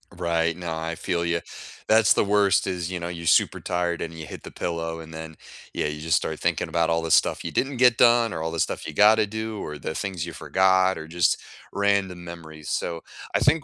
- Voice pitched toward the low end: Yes, very low, 85 Hz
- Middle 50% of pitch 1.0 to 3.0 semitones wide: No, average, 3.4 semitones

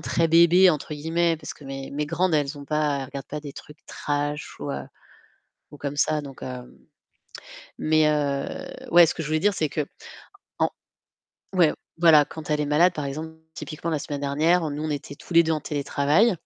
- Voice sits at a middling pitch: Yes, medium, 150 Hz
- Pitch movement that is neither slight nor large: No, narrow, 2.2 semitones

